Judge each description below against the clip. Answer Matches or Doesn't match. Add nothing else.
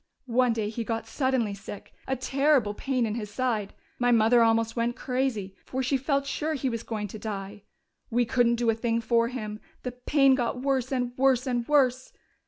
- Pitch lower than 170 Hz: Doesn't match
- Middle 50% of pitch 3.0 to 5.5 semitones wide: Doesn't match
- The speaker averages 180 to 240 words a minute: Matches